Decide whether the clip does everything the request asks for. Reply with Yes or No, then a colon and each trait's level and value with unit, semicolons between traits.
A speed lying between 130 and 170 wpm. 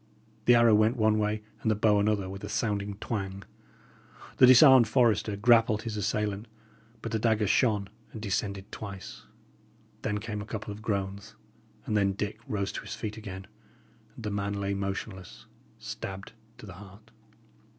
Yes: average, 165 wpm